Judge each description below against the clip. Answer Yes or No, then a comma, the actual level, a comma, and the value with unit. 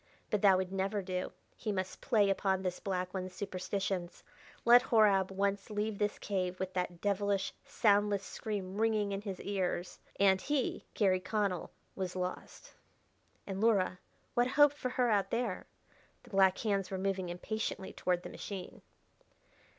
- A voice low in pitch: No, high, 195 Hz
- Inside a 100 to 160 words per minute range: Yes, average, 155 wpm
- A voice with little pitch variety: Yes, narrow, 2.0 semitones